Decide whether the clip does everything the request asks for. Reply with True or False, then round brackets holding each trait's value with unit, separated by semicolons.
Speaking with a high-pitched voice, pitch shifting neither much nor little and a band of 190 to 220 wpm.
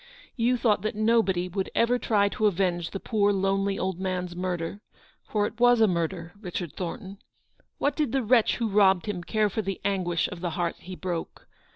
True (195 Hz; 3.3 semitones; 200 wpm)